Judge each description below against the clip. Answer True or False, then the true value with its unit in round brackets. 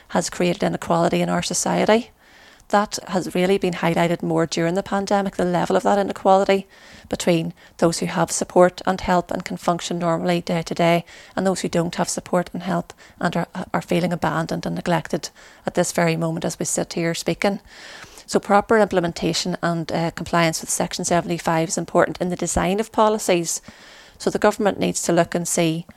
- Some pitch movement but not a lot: False (2.2 semitones)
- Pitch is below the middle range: False (175 Hz)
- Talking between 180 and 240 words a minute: True (190 wpm)